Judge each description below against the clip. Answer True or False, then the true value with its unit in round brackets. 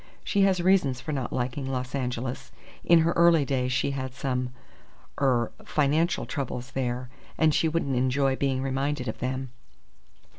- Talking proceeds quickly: False (155 wpm)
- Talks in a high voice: False (135 Hz)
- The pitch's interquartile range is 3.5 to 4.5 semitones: False (3.0 semitones)